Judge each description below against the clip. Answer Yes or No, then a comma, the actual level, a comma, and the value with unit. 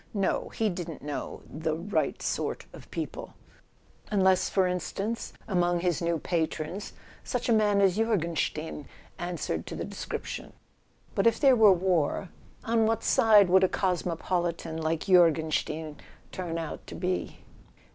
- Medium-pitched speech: Yes, medium, 180 Hz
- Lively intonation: No, average, 3.5 semitones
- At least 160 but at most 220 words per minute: No, average, 145 wpm